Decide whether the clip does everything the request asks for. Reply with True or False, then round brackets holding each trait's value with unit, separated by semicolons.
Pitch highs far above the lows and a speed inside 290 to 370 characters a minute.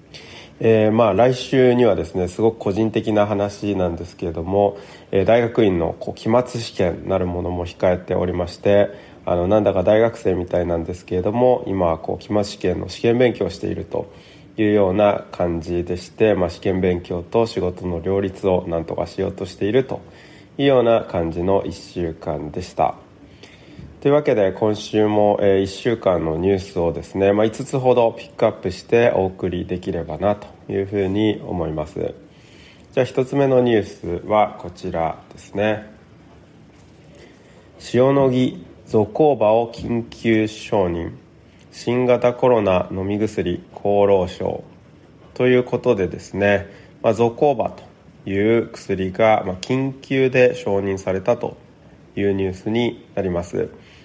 False (4.0 semitones; 300 characters per minute)